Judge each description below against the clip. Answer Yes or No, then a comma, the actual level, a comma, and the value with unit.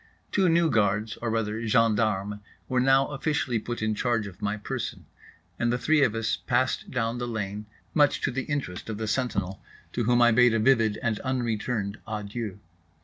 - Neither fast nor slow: Yes, average, 175 wpm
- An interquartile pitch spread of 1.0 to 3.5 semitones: Yes, average, 2.9 semitones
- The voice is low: Yes, low, 115 Hz